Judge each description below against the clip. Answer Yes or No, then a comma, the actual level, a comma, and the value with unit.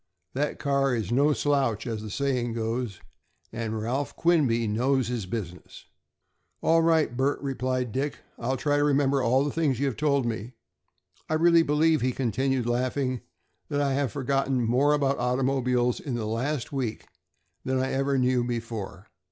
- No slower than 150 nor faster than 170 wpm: Yes, average, 165 wpm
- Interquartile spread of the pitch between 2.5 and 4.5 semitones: Yes, average, 3.0 semitones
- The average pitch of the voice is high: No, low, 130 Hz